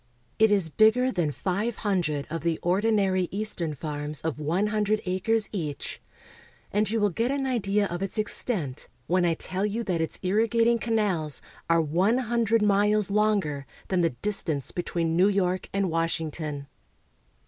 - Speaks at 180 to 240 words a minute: No, average, 160 wpm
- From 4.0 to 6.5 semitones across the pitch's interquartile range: Yes, average, 4.5 semitones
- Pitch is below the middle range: No, high, 190 Hz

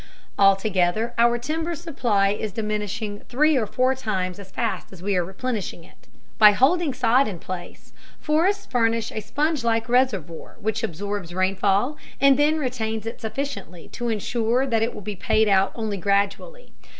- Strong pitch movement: No, average, 4.5 semitones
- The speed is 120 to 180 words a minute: Yes, average, 160 wpm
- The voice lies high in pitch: Yes, high, 220 Hz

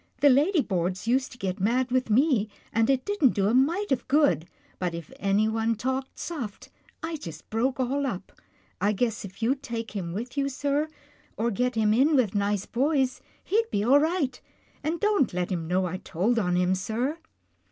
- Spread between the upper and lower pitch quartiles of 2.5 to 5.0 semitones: No, wide, 5.6 semitones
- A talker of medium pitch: No, high, 235 Hz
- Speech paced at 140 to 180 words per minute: No, average, 195 wpm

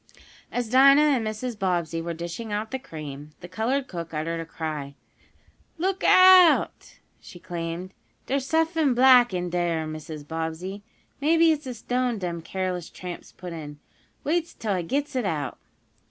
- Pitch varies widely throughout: Yes, wide, 7.9 semitones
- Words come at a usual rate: Yes, average, 155 wpm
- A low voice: No, high, 190 Hz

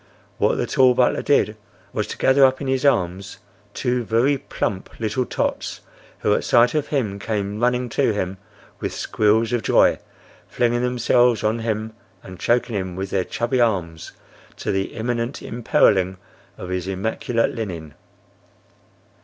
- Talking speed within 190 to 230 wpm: No, average, 155 wpm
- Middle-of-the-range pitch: No, low, 115 Hz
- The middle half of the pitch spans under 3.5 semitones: No, average, 4.0 semitones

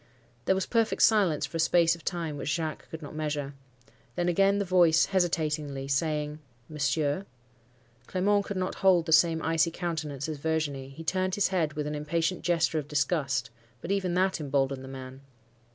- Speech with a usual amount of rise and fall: Yes, average, 3.4 semitones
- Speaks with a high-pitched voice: No, medium, 160 Hz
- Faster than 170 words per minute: Yes, average, 180 wpm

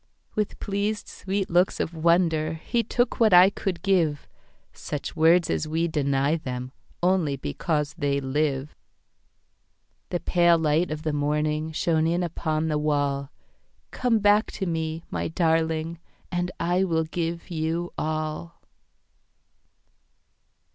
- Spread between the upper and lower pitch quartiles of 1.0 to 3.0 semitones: Yes, narrow, 2.5 semitones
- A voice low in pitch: No, medium, 160 Hz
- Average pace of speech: No, slow, 110 wpm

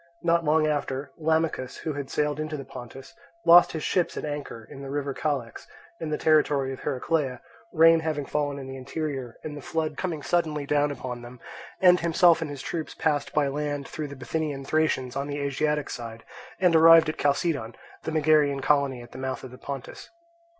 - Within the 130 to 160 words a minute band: No, average, 195 wpm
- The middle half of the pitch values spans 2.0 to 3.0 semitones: Yes, average, 2.7 semitones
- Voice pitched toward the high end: No, medium, 145 Hz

